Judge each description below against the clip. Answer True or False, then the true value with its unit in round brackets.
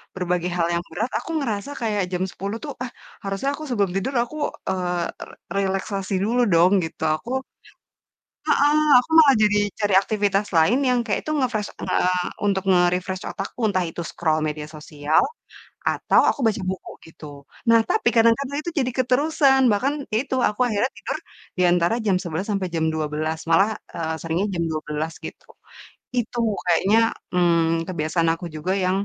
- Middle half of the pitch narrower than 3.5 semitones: False (5.2 semitones)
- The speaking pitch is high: True (195 Hz)